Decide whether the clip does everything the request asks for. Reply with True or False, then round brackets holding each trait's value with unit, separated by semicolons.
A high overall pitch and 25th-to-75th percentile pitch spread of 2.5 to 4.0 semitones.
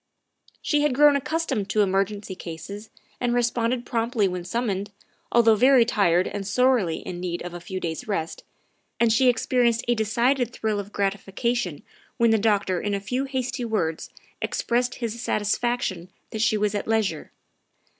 True (220 Hz; 3.7 semitones)